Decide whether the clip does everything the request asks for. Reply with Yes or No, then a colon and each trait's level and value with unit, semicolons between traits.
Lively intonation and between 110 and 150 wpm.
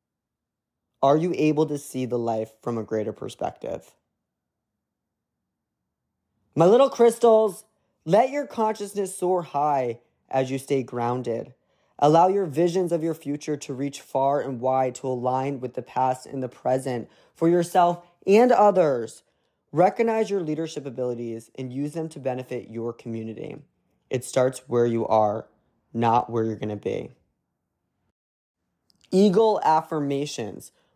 Yes: wide, 6.1 semitones; slow, 135 wpm